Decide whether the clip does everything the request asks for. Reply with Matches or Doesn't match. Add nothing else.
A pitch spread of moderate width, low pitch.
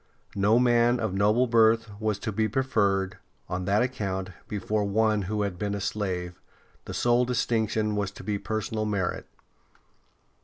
Doesn't match